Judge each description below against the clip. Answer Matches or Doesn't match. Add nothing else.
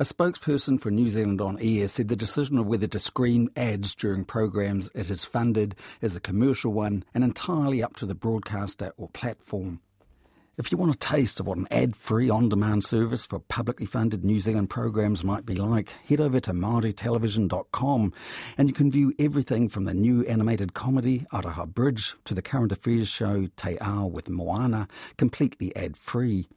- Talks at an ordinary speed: Matches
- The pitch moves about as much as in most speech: Matches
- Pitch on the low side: Matches